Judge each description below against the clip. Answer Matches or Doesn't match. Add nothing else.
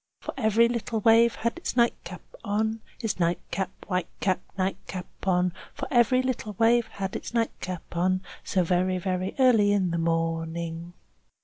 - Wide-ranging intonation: Doesn't match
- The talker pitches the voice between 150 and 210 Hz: Matches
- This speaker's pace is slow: Doesn't match